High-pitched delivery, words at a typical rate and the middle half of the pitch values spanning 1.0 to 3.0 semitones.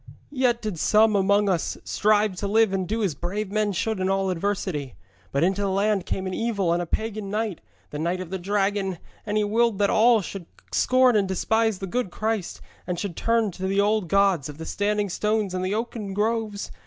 No: high, 200 Hz; fast, 215 wpm; narrow, 2.4 semitones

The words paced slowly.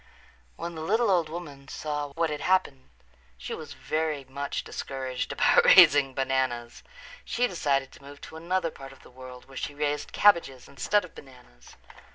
No: average, 170 wpm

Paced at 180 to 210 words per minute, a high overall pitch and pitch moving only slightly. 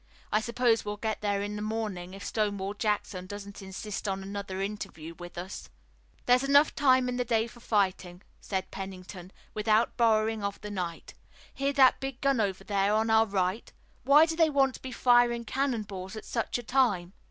No: average, 190 wpm; high, 215 Hz; average, 3.8 semitones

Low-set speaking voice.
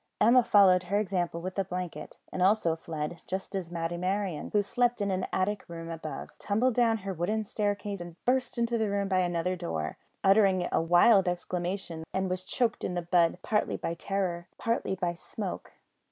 No: medium, 185 Hz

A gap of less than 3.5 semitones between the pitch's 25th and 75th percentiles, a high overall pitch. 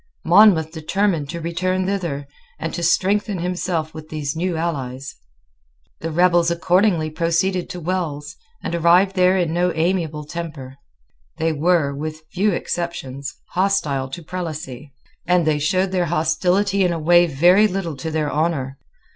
No: average, 2.8 semitones; medium, 170 Hz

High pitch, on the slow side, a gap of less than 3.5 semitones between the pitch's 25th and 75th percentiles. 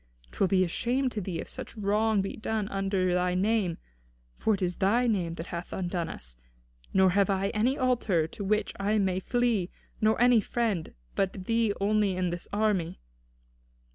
No: high, 195 Hz; average, 180 wpm; average, 3.1 semitones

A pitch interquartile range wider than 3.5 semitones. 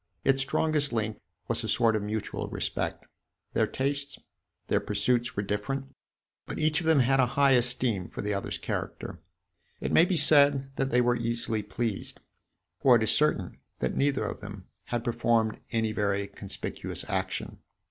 Yes: average, 4.4 semitones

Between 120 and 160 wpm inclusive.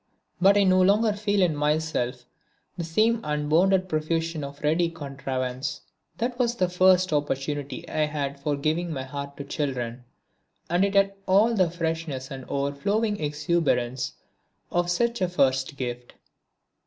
Yes: average, 145 wpm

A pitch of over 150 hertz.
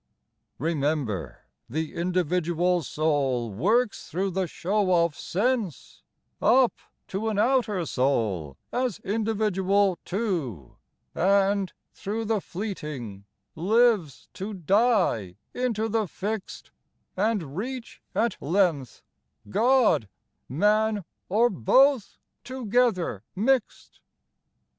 Yes: high, 190 Hz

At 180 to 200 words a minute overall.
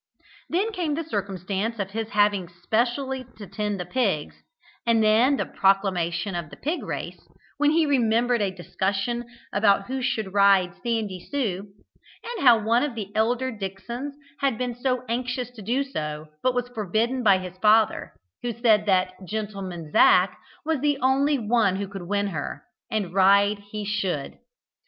No: average, 165 wpm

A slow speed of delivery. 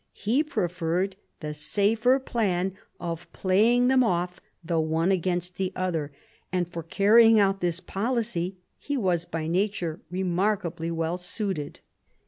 Yes: slow, 130 wpm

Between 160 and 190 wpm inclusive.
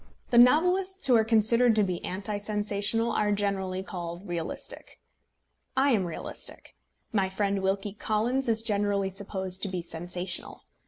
No: average, 145 wpm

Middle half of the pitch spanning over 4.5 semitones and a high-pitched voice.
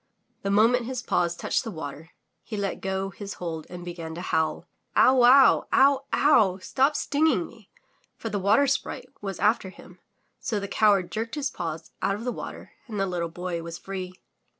Yes: average, 5.2 semitones; high, 195 Hz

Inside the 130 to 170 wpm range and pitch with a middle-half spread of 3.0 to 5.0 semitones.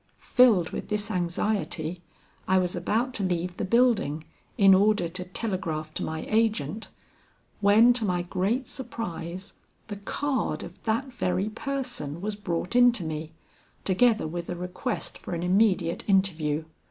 Yes: average, 150 wpm; average, 4.4 semitones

